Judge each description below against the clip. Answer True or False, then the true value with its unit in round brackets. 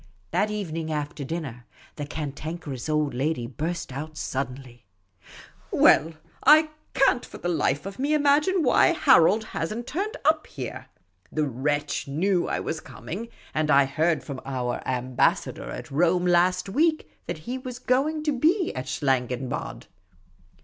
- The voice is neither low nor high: True (160 Hz)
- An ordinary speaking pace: True (150 wpm)